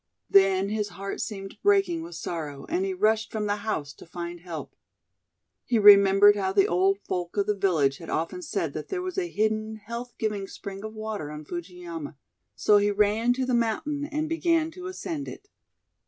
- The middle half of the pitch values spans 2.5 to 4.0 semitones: No, wide, 5.5 semitones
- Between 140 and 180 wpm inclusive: No, average, 190 wpm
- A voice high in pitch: Yes, high, 210 Hz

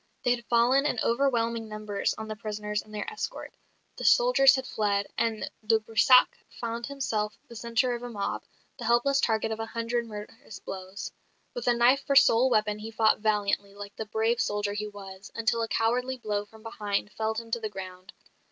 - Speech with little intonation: Yes, narrow, 2.3 semitones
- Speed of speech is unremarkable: Yes, average, 195 wpm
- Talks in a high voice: Yes, high, 225 Hz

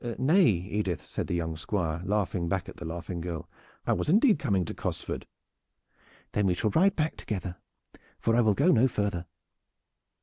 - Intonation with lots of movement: Yes, wide, 5.7 semitones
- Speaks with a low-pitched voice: Yes, low, 100 Hz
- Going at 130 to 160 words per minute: No, average, 175 wpm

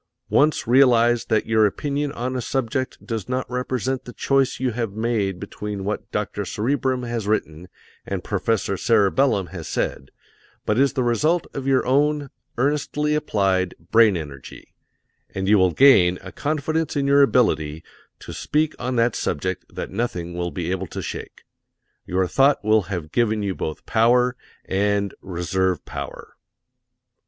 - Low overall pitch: Yes, low, 115 Hz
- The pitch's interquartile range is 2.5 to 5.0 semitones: No, wide, 5.6 semitones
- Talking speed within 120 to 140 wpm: No, average, 155 wpm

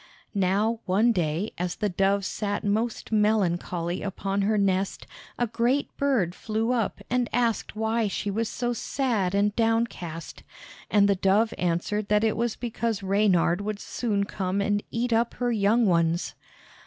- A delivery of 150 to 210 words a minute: Yes, average, 155 wpm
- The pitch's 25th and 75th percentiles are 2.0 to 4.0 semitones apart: Yes, average, 2.9 semitones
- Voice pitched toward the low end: No, high, 210 Hz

